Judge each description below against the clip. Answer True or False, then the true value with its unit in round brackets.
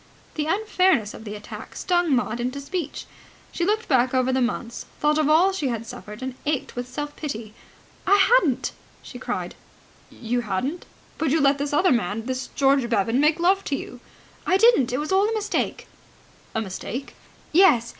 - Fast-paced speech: False (185 wpm)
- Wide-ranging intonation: True (6.2 semitones)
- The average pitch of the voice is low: False (275 Hz)